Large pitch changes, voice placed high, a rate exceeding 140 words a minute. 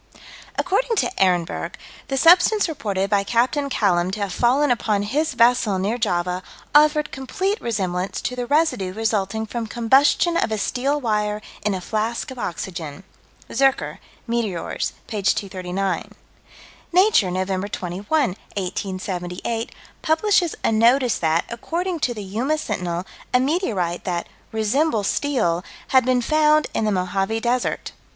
No: wide, 6.5 semitones; high, 225 Hz; slow, 135 wpm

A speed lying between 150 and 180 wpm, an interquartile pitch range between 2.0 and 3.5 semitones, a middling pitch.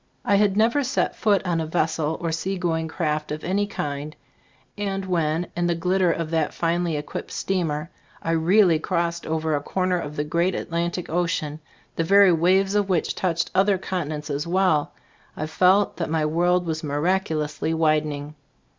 Yes: average, 170 wpm; average, 3.1 semitones; medium, 170 Hz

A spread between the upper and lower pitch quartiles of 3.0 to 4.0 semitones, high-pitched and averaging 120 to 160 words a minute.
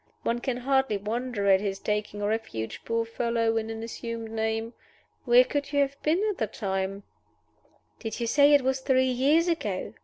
No: average, 3.6 semitones; high, 230 Hz; average, 180 wpm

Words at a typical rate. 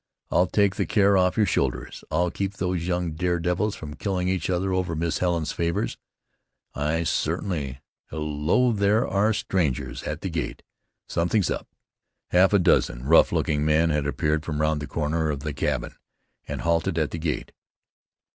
Yes: average, 170 wpm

